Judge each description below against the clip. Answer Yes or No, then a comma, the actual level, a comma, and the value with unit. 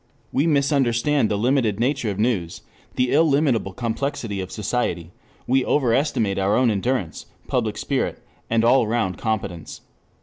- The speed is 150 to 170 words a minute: No, slow, 135 wpm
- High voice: No, low, 115 Hz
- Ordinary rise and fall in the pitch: Yes, average, 4.8 semitones